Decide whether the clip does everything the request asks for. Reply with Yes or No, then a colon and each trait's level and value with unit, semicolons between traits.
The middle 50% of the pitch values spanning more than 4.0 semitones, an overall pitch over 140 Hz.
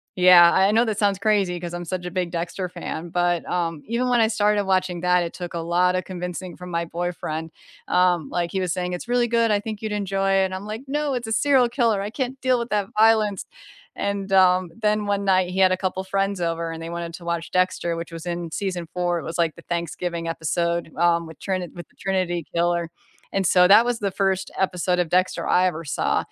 No: average, 2.8 semitones; medium, 185 Hz